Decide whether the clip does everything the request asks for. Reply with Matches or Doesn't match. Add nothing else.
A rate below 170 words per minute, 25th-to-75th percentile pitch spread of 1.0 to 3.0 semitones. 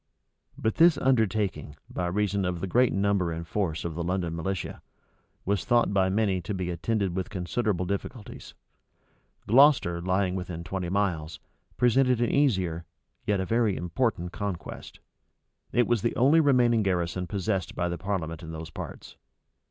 Doesn't match